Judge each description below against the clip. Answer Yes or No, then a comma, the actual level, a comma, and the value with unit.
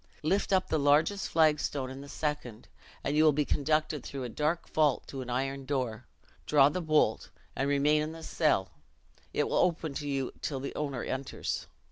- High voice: No, medium, 145 Hz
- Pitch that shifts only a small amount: Yes, narrow, 2.3 semitones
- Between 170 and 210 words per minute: Yes, average, 195 wpm